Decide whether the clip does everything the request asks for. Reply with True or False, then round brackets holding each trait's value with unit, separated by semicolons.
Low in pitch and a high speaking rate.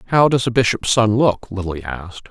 True (110 Hz; 210 wpm)